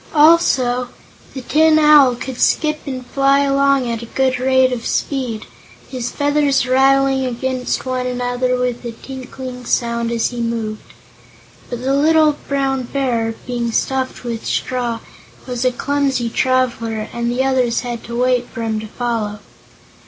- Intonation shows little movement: Yes, narrow, 2.2 semitones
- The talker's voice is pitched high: Yes, very high, 255 Hz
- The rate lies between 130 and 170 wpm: Yes, average, 150 wpm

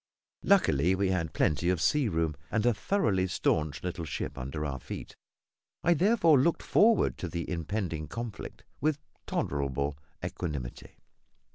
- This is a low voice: Yes, very low, 90 Hz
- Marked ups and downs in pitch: Yes, wide, 7.7 semitones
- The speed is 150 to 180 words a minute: No, average, 140 wpm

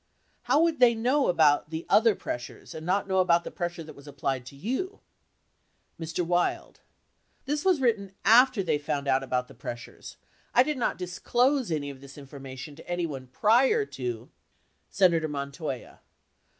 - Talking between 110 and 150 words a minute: No, average, 165 wpm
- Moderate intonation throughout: No, wide, 9.0 semitones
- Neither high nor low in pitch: Yes, medium, 170 Hz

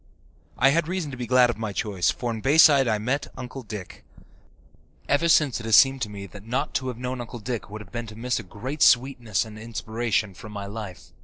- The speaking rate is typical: No, fast, 230 wpm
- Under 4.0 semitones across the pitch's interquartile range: Yes, average, 3.5 semitones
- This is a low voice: Yes, low, 120 Hz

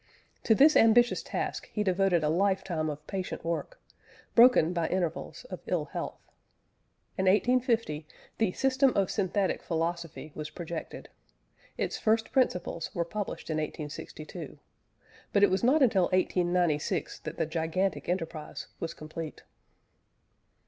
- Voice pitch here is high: No, medium, 180 Hz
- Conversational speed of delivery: No, slow, 130 wpm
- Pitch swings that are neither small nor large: Yes, average, 4.7 semitones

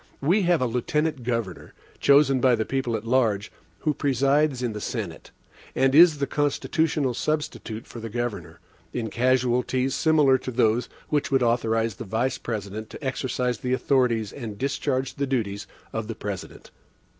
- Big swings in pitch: No, average, 3.5 semitones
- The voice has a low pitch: Yes, low, 125 Hz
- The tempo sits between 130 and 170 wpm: Yes, average, 160 wpm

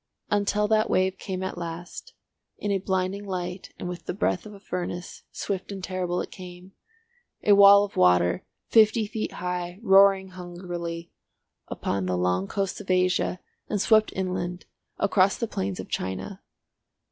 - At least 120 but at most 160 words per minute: Yes, average, 150 wpm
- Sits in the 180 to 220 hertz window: Yes, medium, 185 Hz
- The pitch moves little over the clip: Yes, narrow, 2.3 semitones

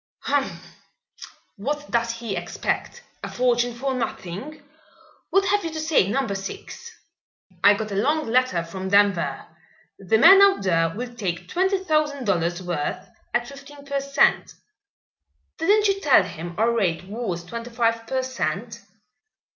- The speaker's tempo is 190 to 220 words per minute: No, average, 145 wpm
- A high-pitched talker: Yes, high, 235 Hz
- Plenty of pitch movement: Yes, wide, 6.7 semitones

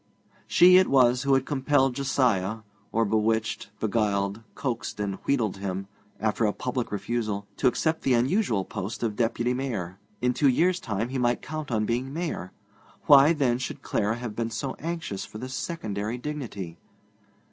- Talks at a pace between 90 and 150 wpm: No, average, 165 wpm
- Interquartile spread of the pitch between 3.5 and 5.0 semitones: Yes, average, 4.3 semitones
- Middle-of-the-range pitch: No, low, 120 Hz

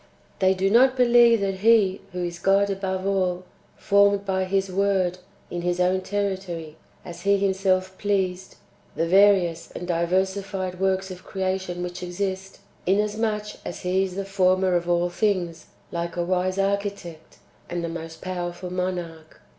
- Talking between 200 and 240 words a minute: No, average, 155 wpm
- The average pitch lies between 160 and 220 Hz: Yes, medium, 185 Hz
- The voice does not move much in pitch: Yes, narrow, 1.9 semitones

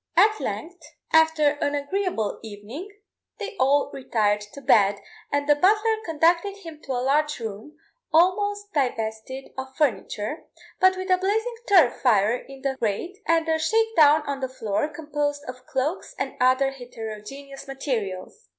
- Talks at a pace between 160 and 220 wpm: No, average, 150 wpm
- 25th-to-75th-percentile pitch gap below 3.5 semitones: No, wide, 5.6 semitones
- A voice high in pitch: Yes, very high, 290 Hz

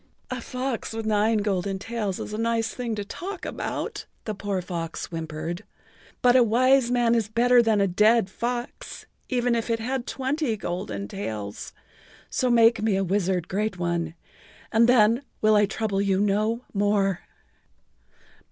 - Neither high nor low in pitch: No, high, 215 Hz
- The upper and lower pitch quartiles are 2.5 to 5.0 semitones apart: Yes, average, 3.5 semitones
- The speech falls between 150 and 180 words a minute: Yes, average, 160 wpm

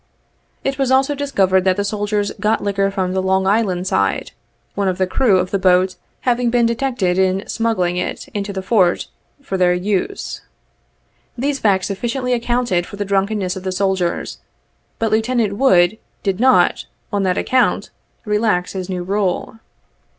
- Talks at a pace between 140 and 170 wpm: Yes, average, 165 wpm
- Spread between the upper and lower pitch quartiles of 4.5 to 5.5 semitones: No, average, 3.6 semitones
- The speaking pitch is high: Yes, high, 200 Hz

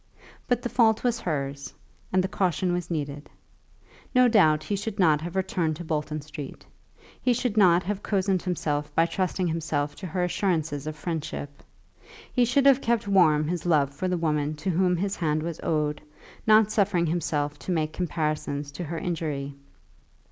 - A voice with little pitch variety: No, average, 4.0 semitones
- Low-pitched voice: No, medium, 170 Hz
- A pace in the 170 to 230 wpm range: Yes, average, 175 wpm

